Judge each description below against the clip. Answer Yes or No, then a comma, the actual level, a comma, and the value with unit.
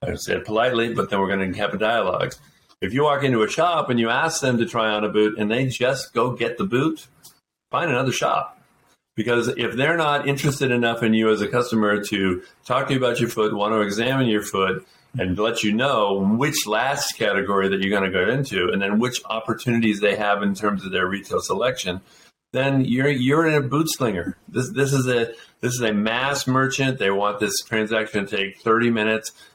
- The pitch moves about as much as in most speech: Yes, average, 4.0 semitones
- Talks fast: Yes, fast, 220 wpm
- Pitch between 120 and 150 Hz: No, low, 110 Hz